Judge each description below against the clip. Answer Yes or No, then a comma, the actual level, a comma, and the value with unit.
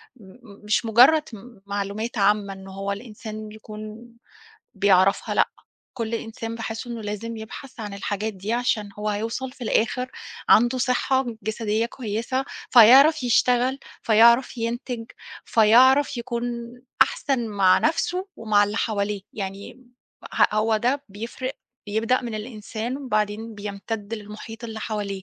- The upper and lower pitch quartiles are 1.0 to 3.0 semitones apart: Yes, narrow, 2.6 semitones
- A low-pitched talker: No, high, 225 Hz